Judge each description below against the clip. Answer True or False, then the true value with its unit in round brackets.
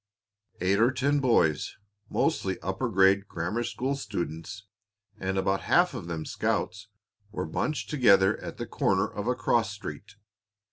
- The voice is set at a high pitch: False (100 Hz)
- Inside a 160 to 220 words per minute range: False (145 wpm)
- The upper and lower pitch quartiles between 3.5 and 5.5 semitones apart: True (4.0 semitones)